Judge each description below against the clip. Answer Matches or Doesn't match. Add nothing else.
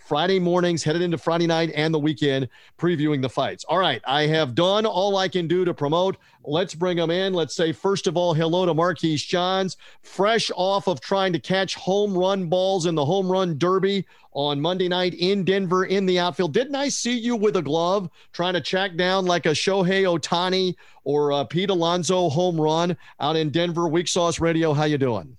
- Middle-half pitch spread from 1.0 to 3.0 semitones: Matches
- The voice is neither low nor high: Matches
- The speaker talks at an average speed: Doesn't match